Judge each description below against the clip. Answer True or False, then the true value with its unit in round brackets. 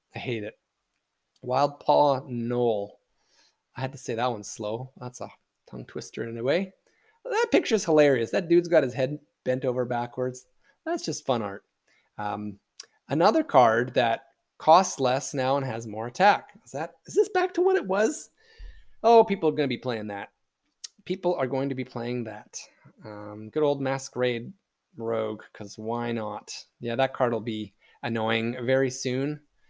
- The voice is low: True (130 Hz)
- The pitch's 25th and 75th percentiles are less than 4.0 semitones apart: False (4.6 semitones)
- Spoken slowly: False (175 wpm)